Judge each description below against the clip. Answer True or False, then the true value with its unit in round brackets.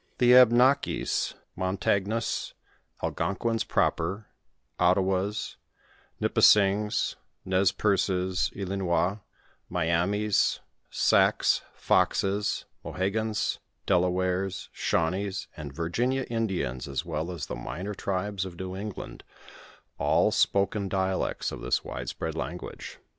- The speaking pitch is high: False (95 Hz)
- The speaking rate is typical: False (95 wpm)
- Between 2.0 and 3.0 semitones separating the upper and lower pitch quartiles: True (2.5 semitones)